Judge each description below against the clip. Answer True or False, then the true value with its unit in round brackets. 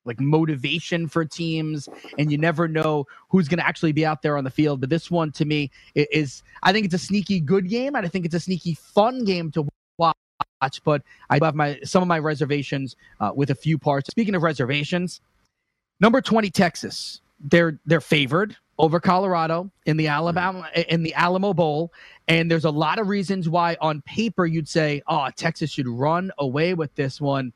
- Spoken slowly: False (200 wpm)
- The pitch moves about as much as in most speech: True (3.2 semitones)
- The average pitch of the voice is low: False (160 Hz)